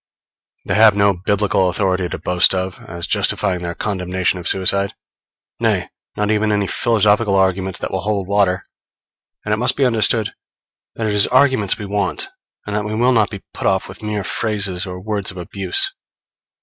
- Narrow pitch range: Yes, narrow, 2.3 semitones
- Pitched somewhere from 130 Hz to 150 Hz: No, low, 100 Hz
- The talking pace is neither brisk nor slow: Yes, average, 180 wpm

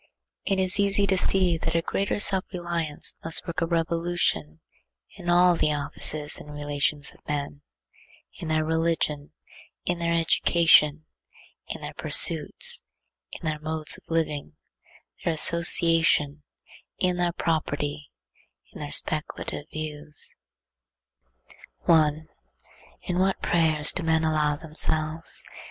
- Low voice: No, medium, 160 Hz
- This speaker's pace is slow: Yes, slow, 120 wpm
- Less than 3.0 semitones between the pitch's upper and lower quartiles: Yes, narrow, 2.4 semitones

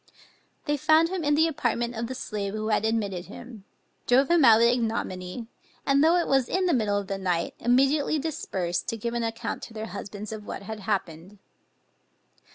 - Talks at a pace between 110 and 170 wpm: No, average, 195 wpm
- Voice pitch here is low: No, high, 230 Hz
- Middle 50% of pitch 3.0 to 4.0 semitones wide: No, average, 5.2 semitones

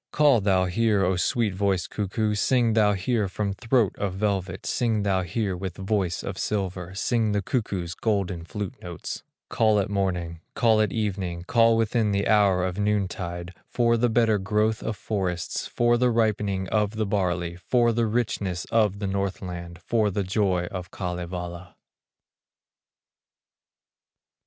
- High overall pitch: No, low, 100 Hz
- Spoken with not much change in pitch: No, average, 3.1 semitones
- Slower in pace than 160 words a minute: Yes, average, 150 wpm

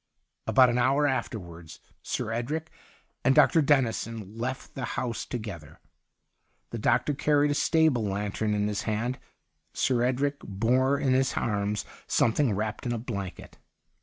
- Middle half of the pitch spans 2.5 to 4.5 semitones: Yes, average, 4.2 semitones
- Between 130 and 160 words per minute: Yes, average, 145 wpm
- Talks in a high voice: No, low, 120 Hz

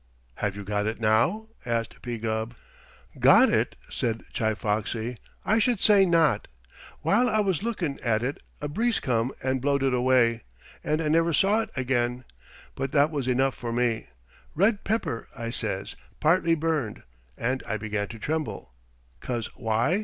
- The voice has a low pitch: Yes, low, 130 Hz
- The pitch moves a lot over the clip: Yes, wide, 6.3 semitones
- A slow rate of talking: No, average, 165 wpm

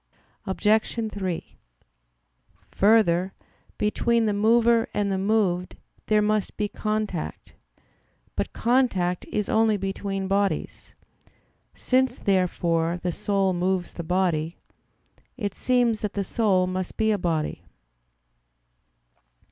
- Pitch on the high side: Yes, high, 200 Hz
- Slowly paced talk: Yes, slow, 110 wpm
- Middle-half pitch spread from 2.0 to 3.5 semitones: Yes, average, 3.1 semitones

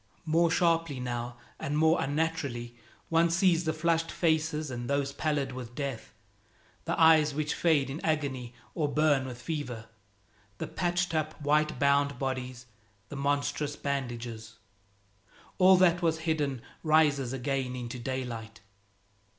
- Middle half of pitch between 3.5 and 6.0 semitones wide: Yes, average, 3.9 semitones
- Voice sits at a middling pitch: Yes, medium, 145 Hz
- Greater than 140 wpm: No, slow, 135 wpm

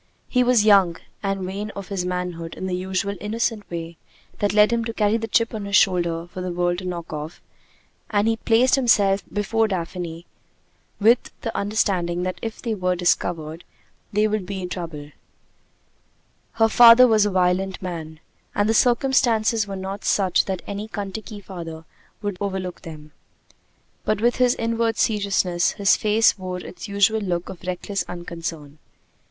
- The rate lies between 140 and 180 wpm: Yes, average, 165 wpm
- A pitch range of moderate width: Yes, average, 3.4 semitones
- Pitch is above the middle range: Yes, high, 195 Hz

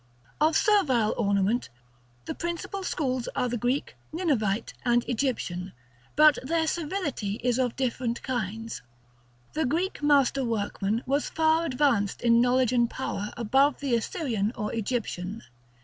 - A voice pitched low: No, very high, 250 Hz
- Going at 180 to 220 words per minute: No, slow, 135 wpm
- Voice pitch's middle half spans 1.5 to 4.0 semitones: No, average, 4.6 semitones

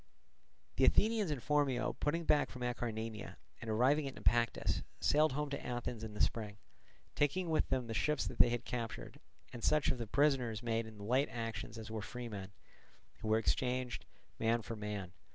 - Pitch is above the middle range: No, low, 120 Hz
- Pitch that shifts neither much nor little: Yes, average, 4.0 semitones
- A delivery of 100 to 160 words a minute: No, average, 185 wpm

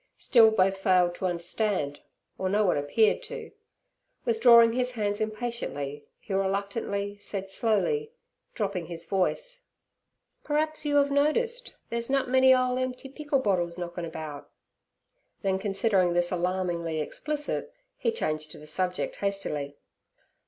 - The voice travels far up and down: Yes, wide, 6.2 semitones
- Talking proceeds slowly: Yes, slow, 130 wpm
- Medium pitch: No, high, 200 Hz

